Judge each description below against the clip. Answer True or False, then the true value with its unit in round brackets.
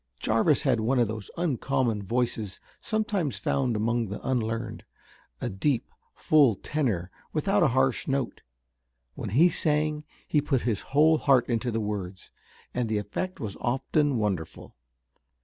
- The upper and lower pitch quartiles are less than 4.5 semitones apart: False (5.3 semitones)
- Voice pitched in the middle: False (125 Hz)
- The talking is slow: False (145 wpm)